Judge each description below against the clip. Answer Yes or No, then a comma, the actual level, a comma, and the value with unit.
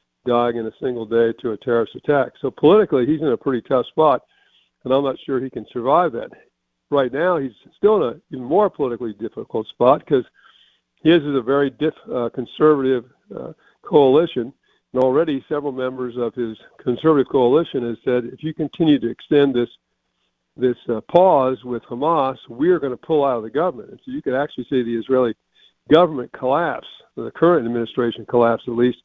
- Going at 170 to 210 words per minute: Yes, average, 190 wpm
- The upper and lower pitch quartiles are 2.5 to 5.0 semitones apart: Yes, average, 3.4 semitones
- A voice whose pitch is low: Yes, low, 125 Hz